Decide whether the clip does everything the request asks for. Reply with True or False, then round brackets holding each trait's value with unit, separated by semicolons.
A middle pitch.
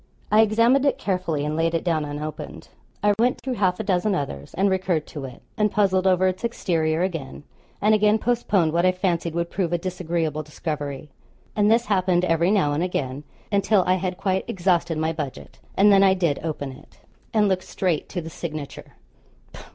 True (180 Hz)